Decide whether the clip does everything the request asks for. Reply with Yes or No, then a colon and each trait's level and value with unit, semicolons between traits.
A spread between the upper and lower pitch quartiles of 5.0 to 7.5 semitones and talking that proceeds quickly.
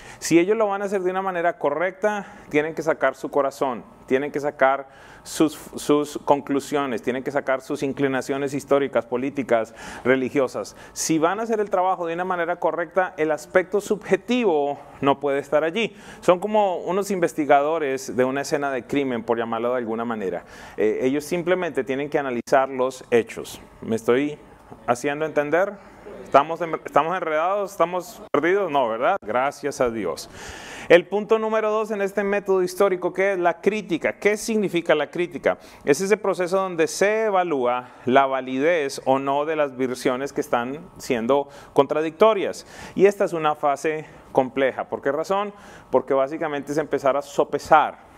No: wide, 5.6 semitones; average, 160 wpm